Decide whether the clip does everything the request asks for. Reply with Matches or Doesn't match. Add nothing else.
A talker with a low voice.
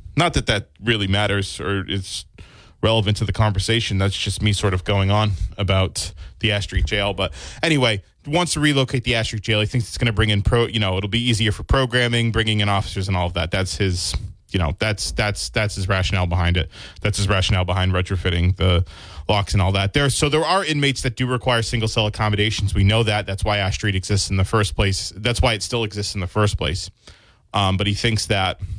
Matches